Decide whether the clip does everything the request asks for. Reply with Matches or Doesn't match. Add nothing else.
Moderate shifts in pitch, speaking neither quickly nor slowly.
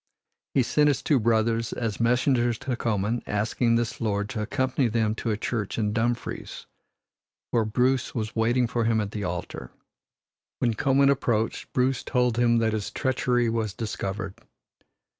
Doesn't match